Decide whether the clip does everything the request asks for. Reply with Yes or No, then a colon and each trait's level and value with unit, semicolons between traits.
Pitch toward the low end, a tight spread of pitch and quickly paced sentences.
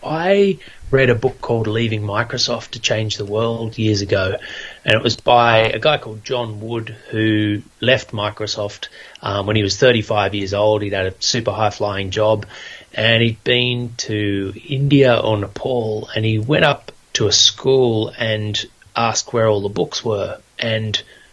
No: low, 110 Hz; narrow, 2.3 semitones; average, 170 wpm